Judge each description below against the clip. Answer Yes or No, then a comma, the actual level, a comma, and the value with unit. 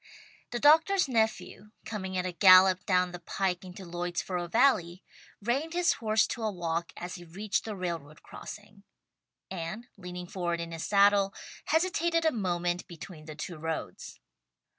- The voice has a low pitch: No, medium, 185 Hz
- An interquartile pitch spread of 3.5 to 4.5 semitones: Yes, average, 4.1 semitones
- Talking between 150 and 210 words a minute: Yes, average, 155 wpm